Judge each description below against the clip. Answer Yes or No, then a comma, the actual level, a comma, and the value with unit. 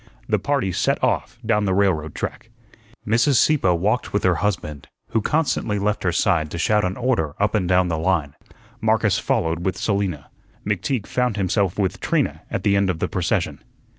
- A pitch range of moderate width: Yes, average, 3.4 semitones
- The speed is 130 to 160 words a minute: No, average, 185 wpm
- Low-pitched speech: Yes, low, 100 Hz